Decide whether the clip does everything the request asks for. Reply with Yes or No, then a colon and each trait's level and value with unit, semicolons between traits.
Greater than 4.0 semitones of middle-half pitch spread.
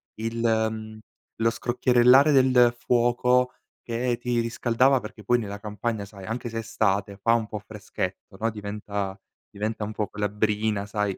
No: narrow, 2.5 semitones